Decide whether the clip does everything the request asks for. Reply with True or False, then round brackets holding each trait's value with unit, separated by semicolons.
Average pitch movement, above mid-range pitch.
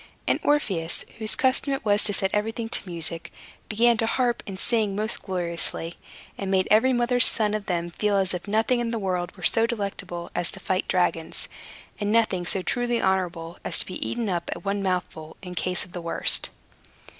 True (4.2 semitones; 195 Hz)